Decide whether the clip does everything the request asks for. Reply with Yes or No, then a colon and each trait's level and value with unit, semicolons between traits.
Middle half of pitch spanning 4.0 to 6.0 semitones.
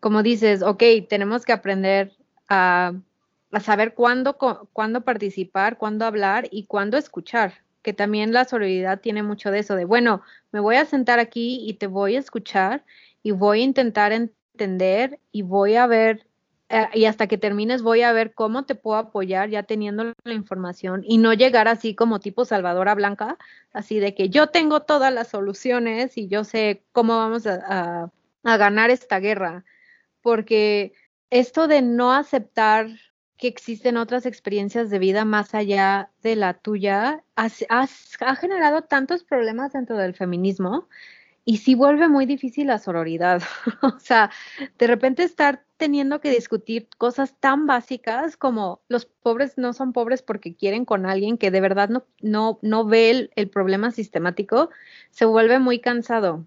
No: average, 3.5 semitones